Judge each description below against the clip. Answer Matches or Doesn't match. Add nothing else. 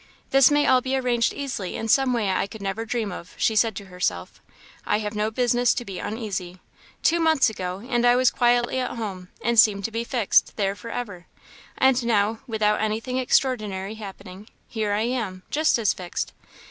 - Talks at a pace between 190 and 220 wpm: Matches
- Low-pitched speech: Doesn't match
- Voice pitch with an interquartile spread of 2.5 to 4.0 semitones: Matches